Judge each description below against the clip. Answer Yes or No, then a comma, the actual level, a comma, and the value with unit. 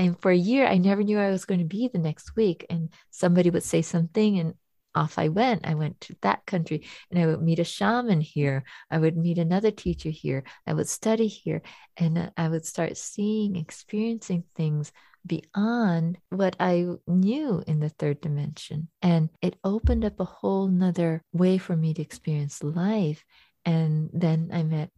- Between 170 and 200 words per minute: Yes, average, 190 wpm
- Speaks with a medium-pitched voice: Yes, medium, 170 Hz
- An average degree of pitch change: Yes, average, 3.3 semitones